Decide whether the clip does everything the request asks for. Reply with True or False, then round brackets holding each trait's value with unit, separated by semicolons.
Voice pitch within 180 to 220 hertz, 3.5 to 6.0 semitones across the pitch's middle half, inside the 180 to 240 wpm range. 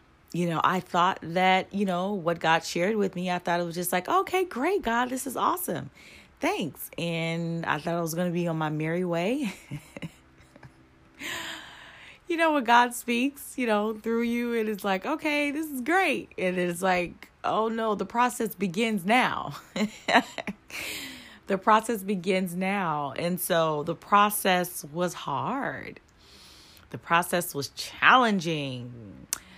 False (185 Hz; 5.5 semitones; 155 wpm)